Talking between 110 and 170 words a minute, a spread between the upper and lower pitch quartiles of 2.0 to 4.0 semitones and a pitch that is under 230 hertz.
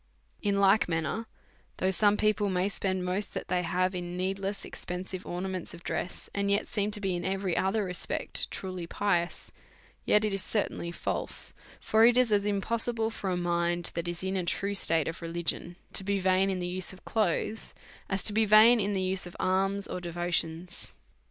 No: average, 195 wpm; narrow, 2.4 semitones; high, 190 Hz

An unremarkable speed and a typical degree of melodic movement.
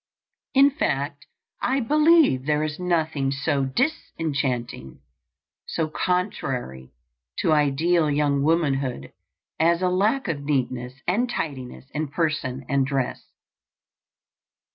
No: slow, 105 wpm; average, 4.5 semitones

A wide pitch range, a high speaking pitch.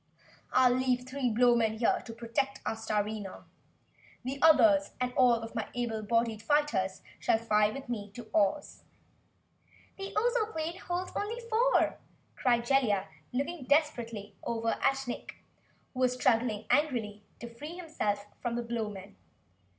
No: average, 4.2 semitones; high, 240 Hz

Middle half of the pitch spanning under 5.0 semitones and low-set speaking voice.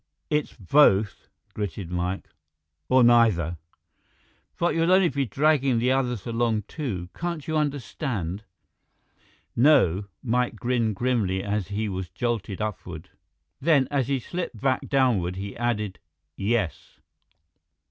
No: wide, 5.6 semitones; low, 115 Hz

